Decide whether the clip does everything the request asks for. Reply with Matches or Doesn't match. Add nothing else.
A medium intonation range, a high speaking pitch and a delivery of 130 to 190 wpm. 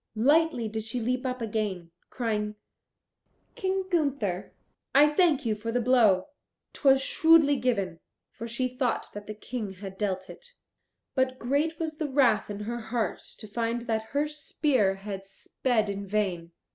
Matches